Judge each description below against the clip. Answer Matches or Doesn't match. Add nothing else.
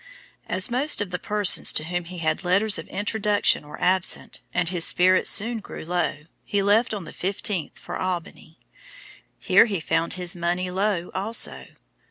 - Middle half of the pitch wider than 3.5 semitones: Doesn't match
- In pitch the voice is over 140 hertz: Matches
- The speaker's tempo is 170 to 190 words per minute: Matches